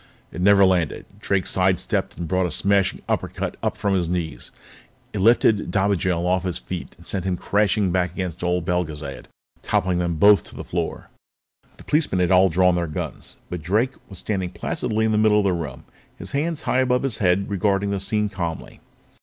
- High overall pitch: No, very low, 95 Hz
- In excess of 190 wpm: Yes, average, 200 wpm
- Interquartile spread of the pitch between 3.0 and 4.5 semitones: No, narrow, 2.5 semitones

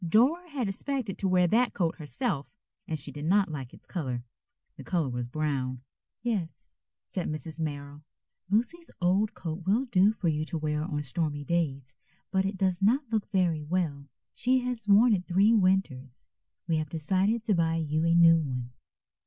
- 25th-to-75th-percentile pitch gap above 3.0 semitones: Yes, average, 5.3 semitones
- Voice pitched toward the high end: No, medium, 170 Hz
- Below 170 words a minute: No, average, 180 wpm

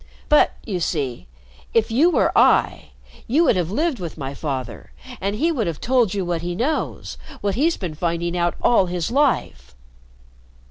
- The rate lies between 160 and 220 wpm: Yes, average, 170 wpm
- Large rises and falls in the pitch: Yes, wide, 7.1 semitones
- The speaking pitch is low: No, medium, 185 Hz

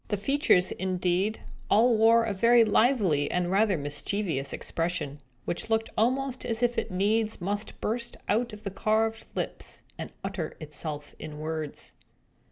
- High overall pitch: Yes, high, 205 Hz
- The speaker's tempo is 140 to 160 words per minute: Yes, average, 150 wpm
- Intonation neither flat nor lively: Yes, average, 4.5 semitones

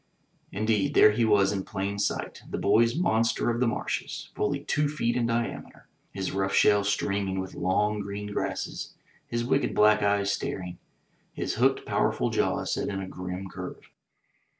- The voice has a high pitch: No, low, 105 Hz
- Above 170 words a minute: No, average, 165 wpm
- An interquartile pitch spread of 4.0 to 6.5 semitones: No, average, 2.9 semitones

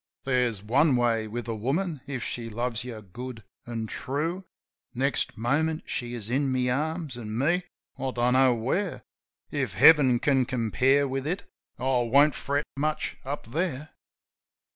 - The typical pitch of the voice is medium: No, low, 130 Hz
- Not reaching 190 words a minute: Yes, average, 155 wpm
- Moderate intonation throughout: Yes, average, 3.4 semitones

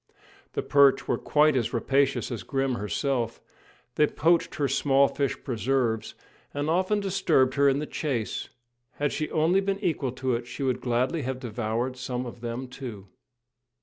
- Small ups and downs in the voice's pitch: No, average, 3.3 semitones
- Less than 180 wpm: Yes, average, 170 wpm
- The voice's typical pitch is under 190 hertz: Yes, low, 135 Hz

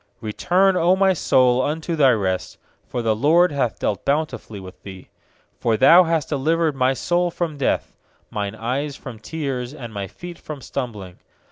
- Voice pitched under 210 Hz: Yes, low, 135 Hz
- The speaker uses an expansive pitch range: Yes, wide, 6.4 semitones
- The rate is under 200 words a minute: Yes, average, 165 wpm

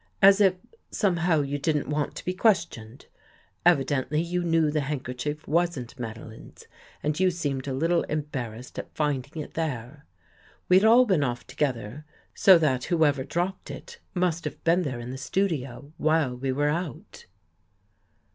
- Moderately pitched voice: Yes, medium, 150 Hz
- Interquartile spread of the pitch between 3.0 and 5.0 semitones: Yes, average, 4.6 semitones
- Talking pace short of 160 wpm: No, average, 165 wpm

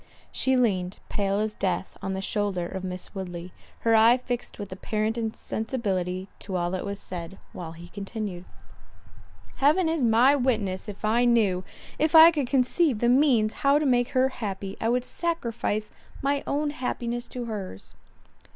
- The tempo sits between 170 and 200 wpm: No, average, 160 wpm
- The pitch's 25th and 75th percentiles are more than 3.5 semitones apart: Yes, average, 4.8 semitones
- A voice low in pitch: No, high, 220 Hz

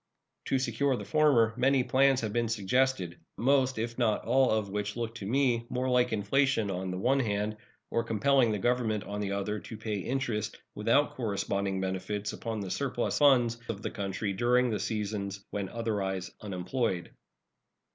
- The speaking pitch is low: Yes, low, 110 Hz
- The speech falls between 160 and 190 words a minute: Yes, average, 170 wpm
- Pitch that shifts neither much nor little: Yes, average, 3.9 semitones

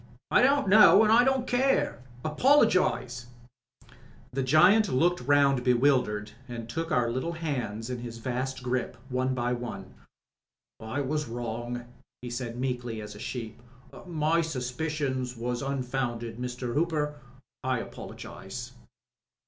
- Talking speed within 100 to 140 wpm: Yes, slow, 135 wpm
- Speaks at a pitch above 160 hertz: No, low, 130 Hz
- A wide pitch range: No, average, 4.4 semitones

